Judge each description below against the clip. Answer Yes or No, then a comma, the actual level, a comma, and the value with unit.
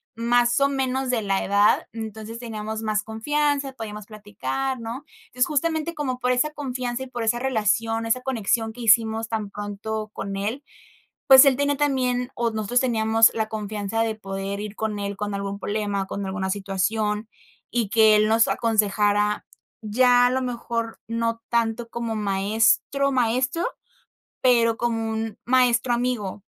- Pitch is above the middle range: Yes, high, 225 Hz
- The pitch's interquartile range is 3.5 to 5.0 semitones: No, average, 3.0 semitones